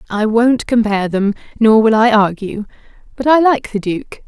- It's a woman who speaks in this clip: Yes, female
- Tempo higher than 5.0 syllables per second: No, 4.9 syllables/s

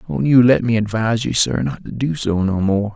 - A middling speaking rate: No, fast, 265 wpm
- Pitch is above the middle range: No, low, 115 Hz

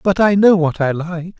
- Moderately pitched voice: Yes, medium, 175 Hz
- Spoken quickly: Yes, fast, 260 wpm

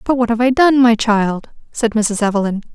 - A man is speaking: No, female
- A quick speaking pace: Yes, fast, 220 wpm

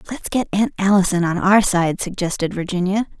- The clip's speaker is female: Yes, female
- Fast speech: No, average, 170 wpm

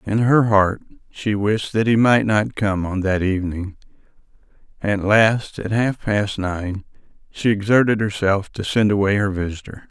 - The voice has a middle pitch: No, low, 105 Hz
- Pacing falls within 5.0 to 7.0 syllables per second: No, 4.4 syllables/s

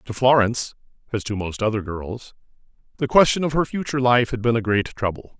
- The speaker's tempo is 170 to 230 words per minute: Yes, average, 200 wpm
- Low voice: Yes, low, 115 Hz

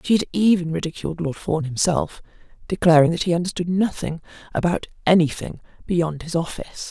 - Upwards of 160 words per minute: No, average, 150 wpm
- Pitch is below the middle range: No, medium, 170 Hz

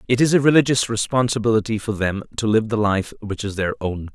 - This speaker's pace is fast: Yes, fast, 215 wpm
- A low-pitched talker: Yes, low, 110 Hz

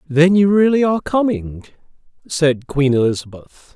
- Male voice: Yes, male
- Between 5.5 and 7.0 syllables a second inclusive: No, 4.7 syllables/s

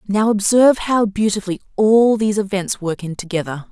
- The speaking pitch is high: Yes, high, 205 Hz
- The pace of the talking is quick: No, average, 160 wpm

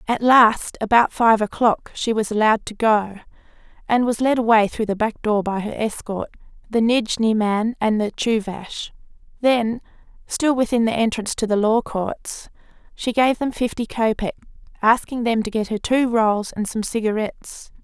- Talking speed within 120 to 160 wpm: No, average, 170 wpm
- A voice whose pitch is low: No, high, 225 Hz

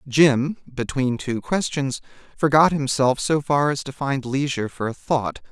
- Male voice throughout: Yes, male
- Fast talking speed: No, average, 165 wpm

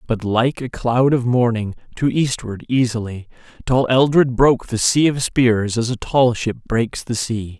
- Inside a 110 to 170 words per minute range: No, average, 180 wpm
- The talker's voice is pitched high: No, low, 120 Hz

